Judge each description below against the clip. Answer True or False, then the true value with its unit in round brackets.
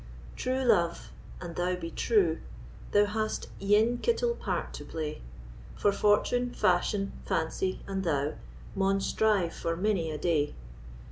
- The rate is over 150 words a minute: False (135 wpm)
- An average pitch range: True (4.3 semitones)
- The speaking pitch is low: False (195 Hz)